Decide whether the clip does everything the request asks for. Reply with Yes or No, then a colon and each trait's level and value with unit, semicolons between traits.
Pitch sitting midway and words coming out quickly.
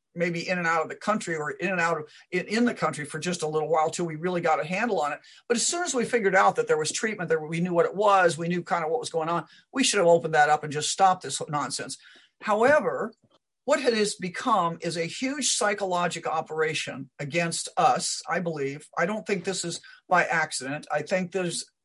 Yes: medium, 175 Hz; fast, 245 wpm